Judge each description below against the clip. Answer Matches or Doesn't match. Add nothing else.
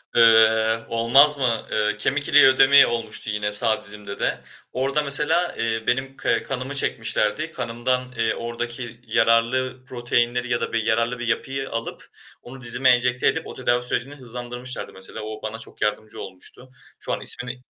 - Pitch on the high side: Doesn't match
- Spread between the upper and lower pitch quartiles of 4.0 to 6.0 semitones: Doesn't match